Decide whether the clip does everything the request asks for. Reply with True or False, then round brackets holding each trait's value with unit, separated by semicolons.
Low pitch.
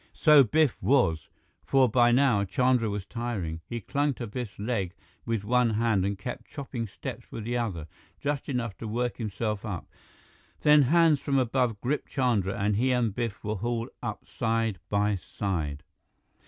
True (115 Hz)